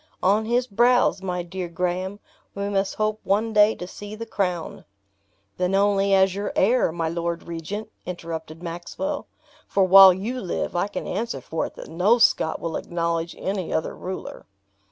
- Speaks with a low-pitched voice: No, high, 190 Hz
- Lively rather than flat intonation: No, average, 3.3 semitones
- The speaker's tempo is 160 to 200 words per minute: Yes, average, 170 wpm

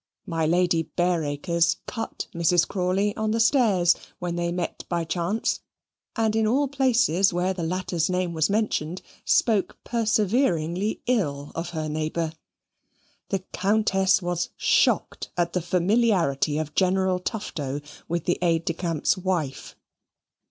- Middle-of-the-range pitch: Yes, medium, 180 Hz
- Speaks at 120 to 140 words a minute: Yes, slow, 135 wpm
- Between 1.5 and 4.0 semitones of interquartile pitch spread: Yes, average, 3.5 semitones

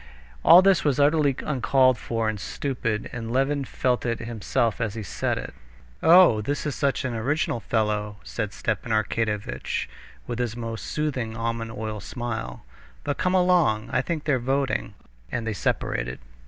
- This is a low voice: Yes, low, 120 Hz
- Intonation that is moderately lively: Yes, average, 4.2 semitones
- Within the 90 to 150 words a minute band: No, average, 160 wpm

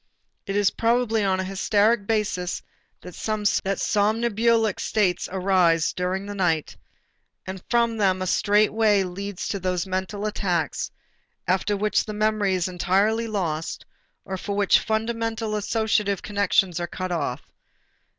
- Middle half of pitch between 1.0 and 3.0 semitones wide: Yes, narrow, 2.6 semitones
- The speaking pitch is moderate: No, high, 200 Hz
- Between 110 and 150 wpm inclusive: Yes, average, 140 wpm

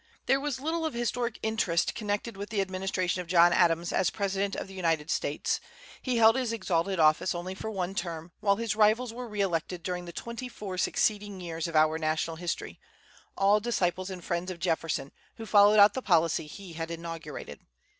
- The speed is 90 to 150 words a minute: No, average, 195 wpm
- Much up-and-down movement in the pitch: No, average, 4.1 semitones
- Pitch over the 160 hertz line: Yes, high, 190 Hz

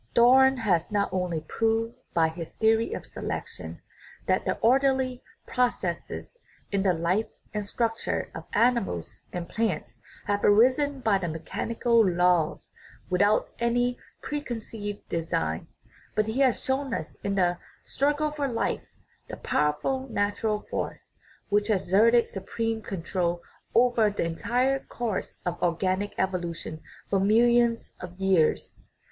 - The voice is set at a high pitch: Yes, high, 210 Hz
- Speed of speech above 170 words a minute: No, slow, 135 wpm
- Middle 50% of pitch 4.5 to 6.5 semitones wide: Yes, average, 5.1 semitones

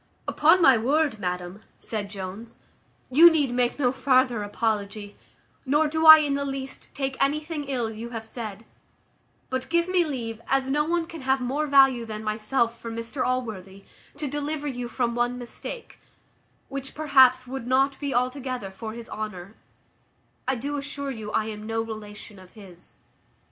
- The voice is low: No, very high, 250 Hz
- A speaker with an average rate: Yes, average, 165 wpm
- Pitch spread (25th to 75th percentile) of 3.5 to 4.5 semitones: Yes, average, 4.2 semitones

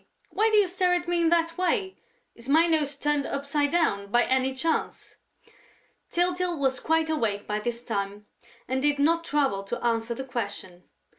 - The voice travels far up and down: Yes, wide, 6.1 semitones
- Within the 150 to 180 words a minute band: Yes, average, 175 wpm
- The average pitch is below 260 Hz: No, very high, 285 Hz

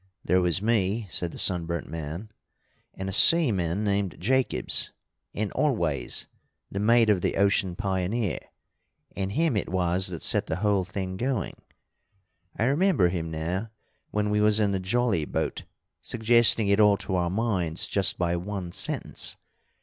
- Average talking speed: Yes, average, 155 wpm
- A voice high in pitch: No, low, 100 Hz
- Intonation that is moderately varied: Yes, average, 3.4 semitones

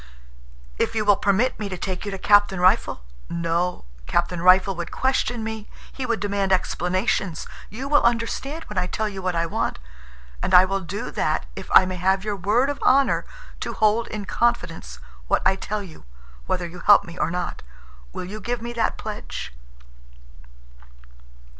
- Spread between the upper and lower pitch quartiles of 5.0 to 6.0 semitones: No, average, 3.6 semitones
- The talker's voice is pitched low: No, high, 195 Hz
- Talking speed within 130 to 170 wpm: No, average, 180 wpm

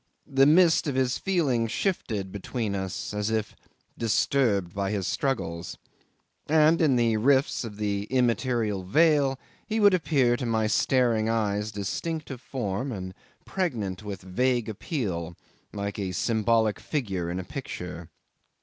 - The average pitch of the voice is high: No, low, 115 Hz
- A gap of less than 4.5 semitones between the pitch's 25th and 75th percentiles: No, average, 5.1 semitones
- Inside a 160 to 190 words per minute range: No, average, 140 wpm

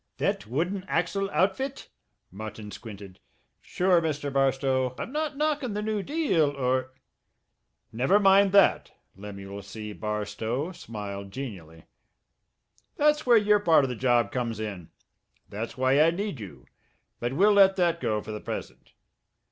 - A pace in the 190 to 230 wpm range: No, average, 145 wpm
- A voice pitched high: No, low, 135 Hz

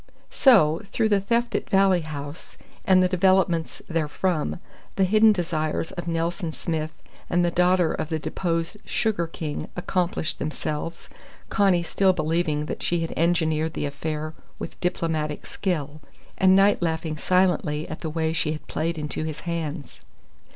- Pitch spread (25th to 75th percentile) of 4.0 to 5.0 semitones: No, average, 2.8 semitones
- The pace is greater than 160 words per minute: No, average, 150 wpm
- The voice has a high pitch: No, medium, 165 Hz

